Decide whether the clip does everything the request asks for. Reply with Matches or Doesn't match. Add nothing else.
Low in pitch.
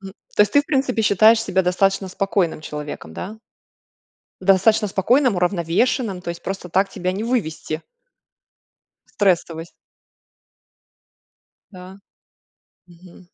Doesn't match